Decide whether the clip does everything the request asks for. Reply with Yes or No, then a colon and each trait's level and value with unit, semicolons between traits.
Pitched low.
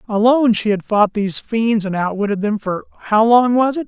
No: high, 215 Hz